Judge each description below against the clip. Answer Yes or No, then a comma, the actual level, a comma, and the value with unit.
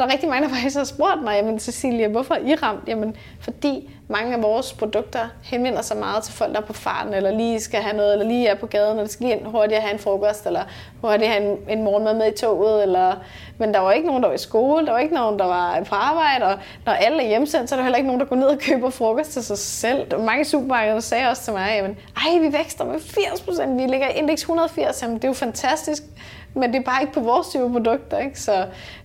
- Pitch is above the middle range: Yes, high, 235 Hz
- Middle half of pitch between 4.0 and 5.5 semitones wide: Yes, average, 4.4 semitones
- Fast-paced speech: Yes, fast, 275 wpm